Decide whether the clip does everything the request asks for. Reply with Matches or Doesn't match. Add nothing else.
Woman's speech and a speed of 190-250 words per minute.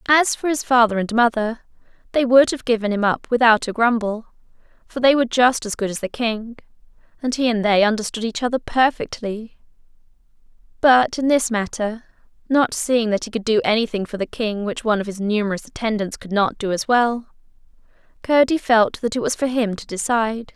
Matches